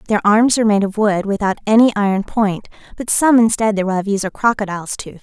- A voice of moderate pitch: No, high, 210 Hz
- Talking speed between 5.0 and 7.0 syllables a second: Yes, 5.9 syllables/s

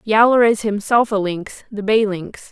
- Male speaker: No, female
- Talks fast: No, average, 190 wpm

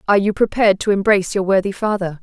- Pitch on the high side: Yes, high, 200 Hz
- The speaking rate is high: Yes, fast, 215 wpm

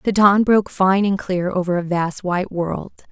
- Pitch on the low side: No, high, 190 Hz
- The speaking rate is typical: No, fast, 210 wpm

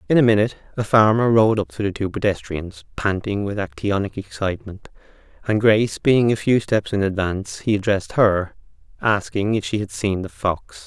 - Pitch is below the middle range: Yes, low, 105 Hz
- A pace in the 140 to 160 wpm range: No, average, 180 wpm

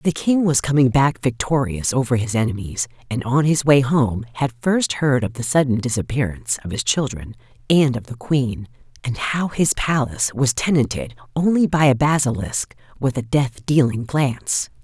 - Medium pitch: No, low, 130 Hz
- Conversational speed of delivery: Yes, average, 175 wpm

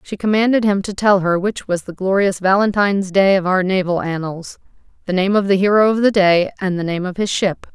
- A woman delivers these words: Yes, female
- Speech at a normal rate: No, fast, 230 wpm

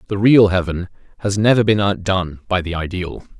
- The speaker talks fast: No, average, 175 wpm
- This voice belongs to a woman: No, male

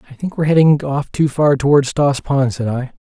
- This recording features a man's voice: Yes, male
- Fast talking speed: Yes, fast, 235 wpm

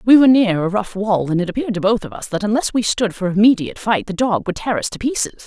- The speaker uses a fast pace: Yes, fast, 295 wpm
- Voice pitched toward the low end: No, high, 210 Hz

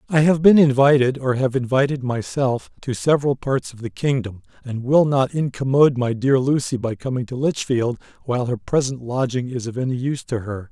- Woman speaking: No, male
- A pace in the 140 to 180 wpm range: No, average, 195 wpm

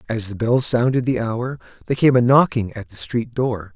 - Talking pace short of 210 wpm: No, fast, 225 wpm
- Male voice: Yes, male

